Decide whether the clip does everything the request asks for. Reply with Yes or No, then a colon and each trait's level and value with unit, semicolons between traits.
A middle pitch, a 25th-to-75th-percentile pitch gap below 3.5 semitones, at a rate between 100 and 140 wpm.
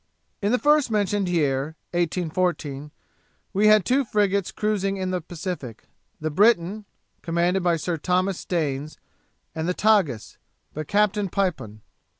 No: medium, 180 Hz; average, 4.4 semitones; slow, 135 wpm